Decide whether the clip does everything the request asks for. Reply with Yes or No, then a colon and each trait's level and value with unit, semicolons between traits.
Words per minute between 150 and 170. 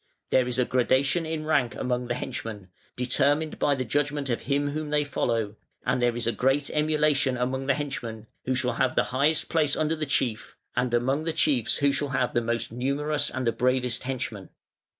No: average, 200 wpm